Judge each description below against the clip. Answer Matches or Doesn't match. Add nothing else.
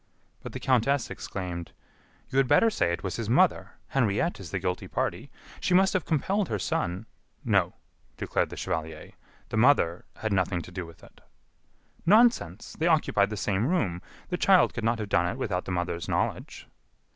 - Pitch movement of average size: Doesn't match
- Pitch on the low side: Matches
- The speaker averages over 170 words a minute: Matches